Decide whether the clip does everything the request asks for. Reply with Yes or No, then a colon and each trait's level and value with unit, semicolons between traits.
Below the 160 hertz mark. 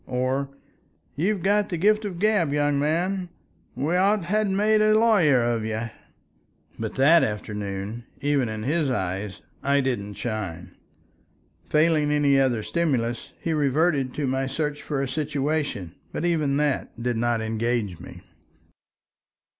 Yes: medium, 140 Hz